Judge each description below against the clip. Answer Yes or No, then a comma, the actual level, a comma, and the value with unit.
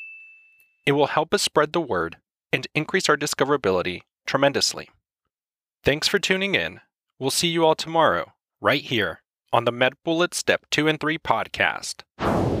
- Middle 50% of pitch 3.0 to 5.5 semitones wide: Yes, average, 3.4 semitones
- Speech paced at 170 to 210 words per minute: No, average, 150 wpm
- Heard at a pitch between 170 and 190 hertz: No, medium, 155 Hz